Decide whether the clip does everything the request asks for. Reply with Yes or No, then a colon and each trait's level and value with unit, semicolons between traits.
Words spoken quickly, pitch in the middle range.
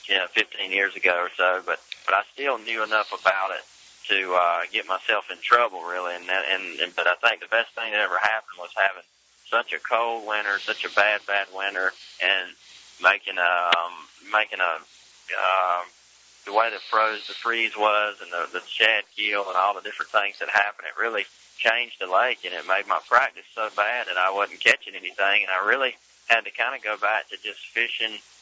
No: fast, 210 wpm; low, 105 Hz